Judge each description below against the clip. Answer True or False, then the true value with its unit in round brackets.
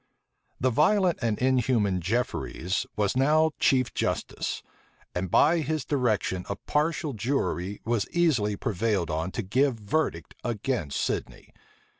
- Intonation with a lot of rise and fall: True (6.2 semitones)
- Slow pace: True (125 wpm)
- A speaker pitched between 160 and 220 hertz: False (120 Hz)